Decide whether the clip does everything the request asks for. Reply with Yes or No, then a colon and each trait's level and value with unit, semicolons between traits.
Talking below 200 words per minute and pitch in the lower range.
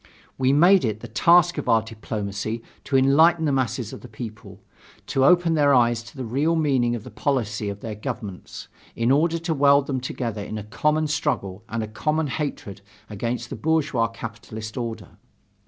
Yes: average, 185 wpm; low, 125 Hz